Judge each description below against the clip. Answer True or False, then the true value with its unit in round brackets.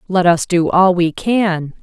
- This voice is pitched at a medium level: True (180 Hz)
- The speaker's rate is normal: True (195 wpm)